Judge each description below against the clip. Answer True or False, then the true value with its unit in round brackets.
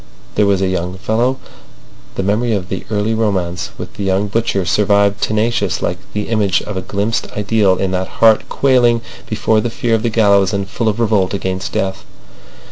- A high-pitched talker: False (105 Hz)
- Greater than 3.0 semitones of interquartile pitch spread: False (2.7 semitones)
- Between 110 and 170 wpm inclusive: False (190 wpm)